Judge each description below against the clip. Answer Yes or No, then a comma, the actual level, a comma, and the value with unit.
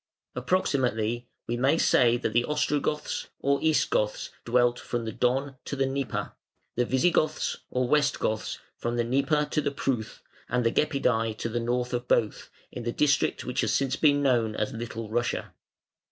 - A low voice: Yes, low, 125 Hz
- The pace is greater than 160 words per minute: Yes, average, 175 wpm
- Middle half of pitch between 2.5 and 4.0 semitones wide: Yes, average, 2.9 semitones